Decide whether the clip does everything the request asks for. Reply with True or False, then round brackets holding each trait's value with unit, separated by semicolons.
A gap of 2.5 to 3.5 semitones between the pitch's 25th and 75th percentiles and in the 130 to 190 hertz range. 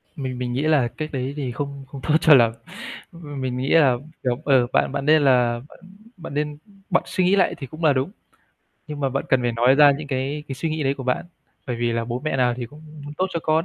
True (3.1 semitones; 135 Hz)